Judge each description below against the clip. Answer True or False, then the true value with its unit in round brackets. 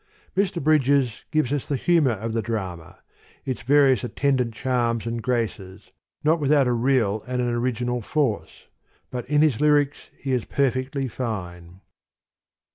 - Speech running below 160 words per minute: True (150 wpm)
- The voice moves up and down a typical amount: True (3.7 semitones)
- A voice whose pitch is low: True (125 Hz)